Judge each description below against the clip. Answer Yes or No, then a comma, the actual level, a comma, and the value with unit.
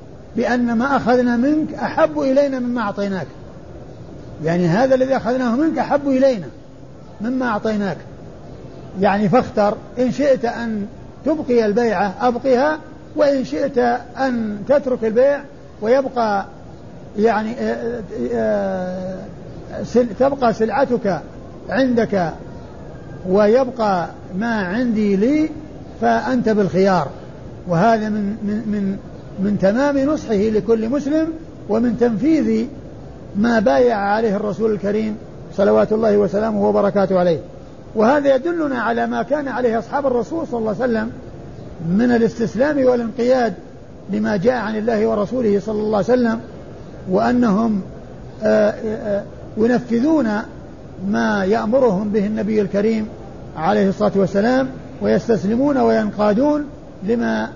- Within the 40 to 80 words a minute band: No, average, 105 wpm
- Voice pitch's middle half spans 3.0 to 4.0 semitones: Yes, average, 3.5 semitones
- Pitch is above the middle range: Yes, high, 225 Hz